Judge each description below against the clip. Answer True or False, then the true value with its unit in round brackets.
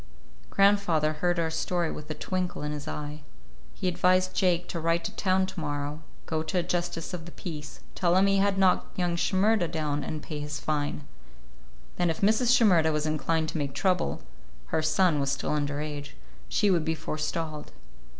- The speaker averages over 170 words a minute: True (180 wpm)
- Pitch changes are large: False (3.4 semitones)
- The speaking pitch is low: False (160 Hz)